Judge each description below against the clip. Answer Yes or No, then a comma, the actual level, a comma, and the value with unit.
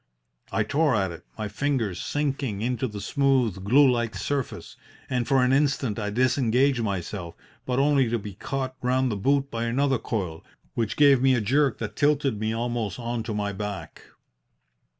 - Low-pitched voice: Yes, low, 120 Hz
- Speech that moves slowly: No, average, 175 wpm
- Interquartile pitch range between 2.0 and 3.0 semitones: No, average, 4.4 semitones